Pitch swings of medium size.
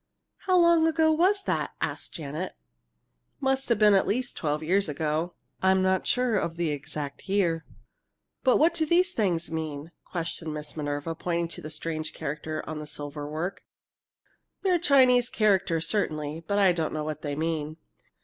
No: wide, 7.3 semitones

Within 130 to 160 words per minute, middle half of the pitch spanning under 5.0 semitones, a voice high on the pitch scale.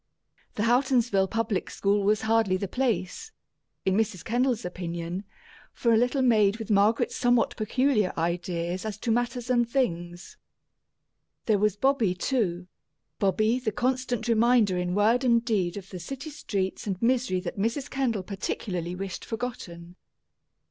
Yes: average, 145 wpm; average, 4.6 semitones; high, 215 Hz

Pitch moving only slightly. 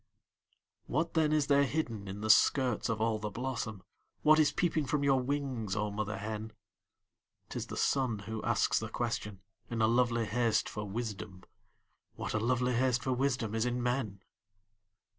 No: average, 3.6 semitones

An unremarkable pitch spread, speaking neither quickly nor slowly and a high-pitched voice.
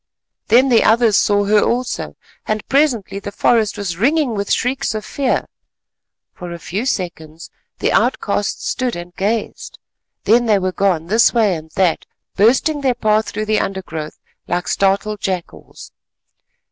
Yes: average, 4.0 semitones; average, 150 wpm; high, 210 Hz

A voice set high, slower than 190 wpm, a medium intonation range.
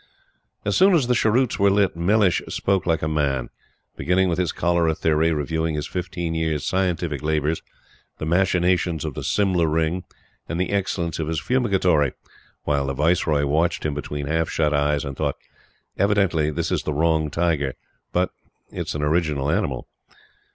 No: very low, 80 Hz; average, 170 wpm; average, 3.2 semitones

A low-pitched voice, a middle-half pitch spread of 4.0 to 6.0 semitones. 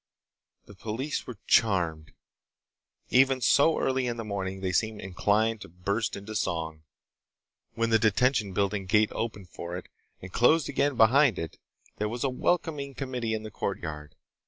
Yes: low, 110 Hz; average, 4.9 semitones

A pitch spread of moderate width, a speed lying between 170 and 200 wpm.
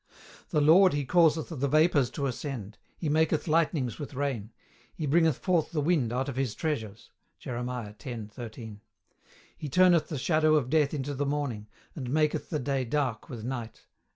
Yes: average, 4.1 semitones; average, 175 wpm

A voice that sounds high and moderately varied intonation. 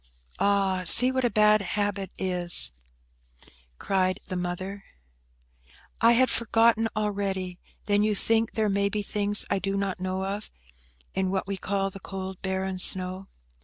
No: high, 195 Hz; narrow, 1.9 semitones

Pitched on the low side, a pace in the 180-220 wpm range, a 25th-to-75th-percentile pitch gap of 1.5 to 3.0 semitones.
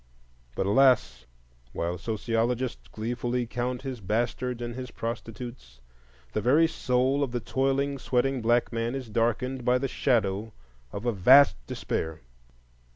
No: low, 120 Hz; slow, 135 wpm; narrow, 2.5 semitones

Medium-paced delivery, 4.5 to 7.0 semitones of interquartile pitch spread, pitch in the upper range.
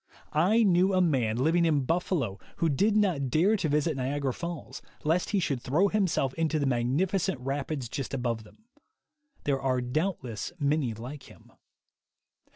No: average, 160 wpm; average, 5.3 semitones; medium, 150 Hz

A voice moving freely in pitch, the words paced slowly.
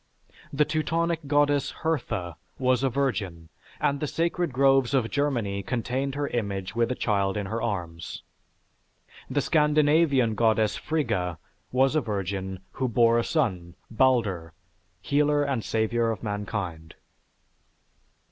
Yes: wide, 6.1 semitones; slow, 130 wpm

